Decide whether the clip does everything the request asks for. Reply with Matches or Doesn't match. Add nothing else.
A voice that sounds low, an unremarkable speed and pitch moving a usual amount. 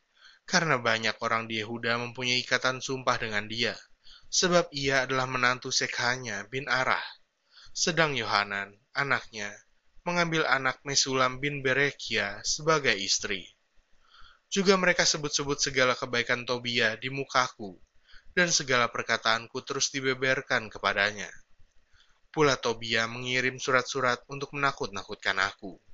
Matches